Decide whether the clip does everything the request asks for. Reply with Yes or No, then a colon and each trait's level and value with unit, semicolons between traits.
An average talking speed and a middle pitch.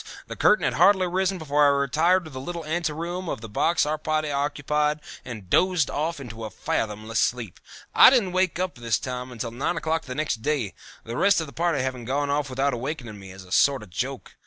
No: fast, 225 wpm; medium, 145 Hz